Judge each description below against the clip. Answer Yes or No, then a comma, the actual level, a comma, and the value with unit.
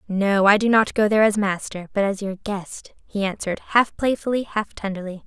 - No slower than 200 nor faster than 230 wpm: Yes, fast, 205 wpm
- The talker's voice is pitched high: Yes, high, 205 Hz